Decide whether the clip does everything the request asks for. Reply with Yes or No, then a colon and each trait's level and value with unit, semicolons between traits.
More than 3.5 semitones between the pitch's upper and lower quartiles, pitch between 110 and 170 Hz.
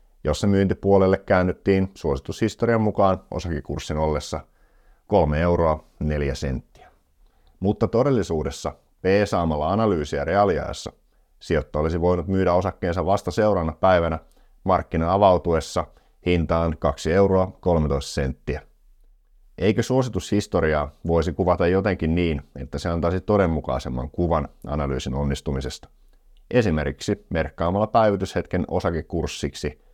No: average, 4.1 semitones; very low, 85 Hz